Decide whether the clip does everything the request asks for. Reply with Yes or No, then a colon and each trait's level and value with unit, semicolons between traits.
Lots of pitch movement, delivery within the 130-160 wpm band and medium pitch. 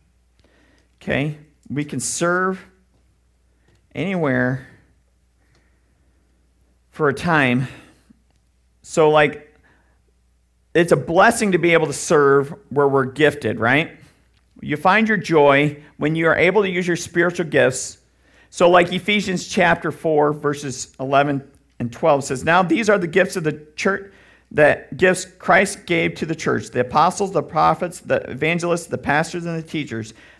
Yes: wide, 6.6 semitones; average, 140 wpm; medium, 150 Hz